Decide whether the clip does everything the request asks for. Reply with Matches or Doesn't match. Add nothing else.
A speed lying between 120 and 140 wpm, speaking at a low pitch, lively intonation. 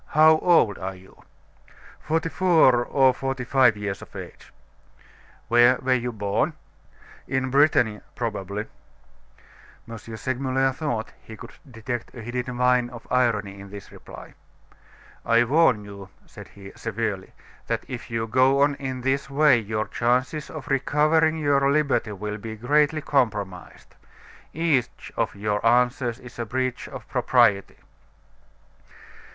Doesn't match